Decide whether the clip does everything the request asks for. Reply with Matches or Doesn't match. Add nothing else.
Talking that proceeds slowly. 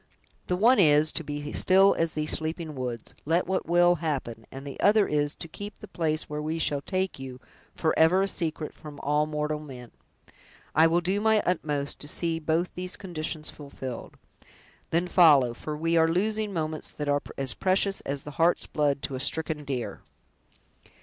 Doesn't match